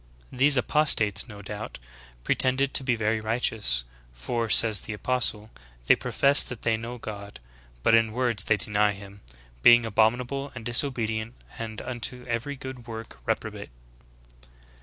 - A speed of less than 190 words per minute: Yes, average, 145 wpm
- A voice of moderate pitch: No, low, 115 Hz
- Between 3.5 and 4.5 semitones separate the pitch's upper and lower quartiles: No, average, 2.7 semitones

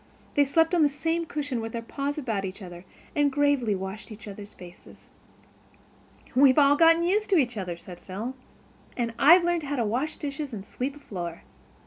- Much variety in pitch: Yes, wide, 6.1 semitones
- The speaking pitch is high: Yes, very high, 270 Hz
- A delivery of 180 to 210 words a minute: Yes, average, 190 wpm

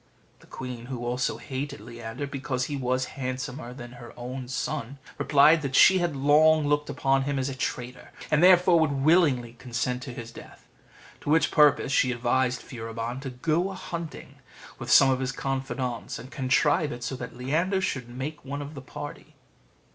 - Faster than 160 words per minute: Yes, average, 180 wpm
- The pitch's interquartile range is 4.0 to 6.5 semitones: No, average, 2.9 semitones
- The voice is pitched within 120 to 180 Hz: Yes, low, 135 Hz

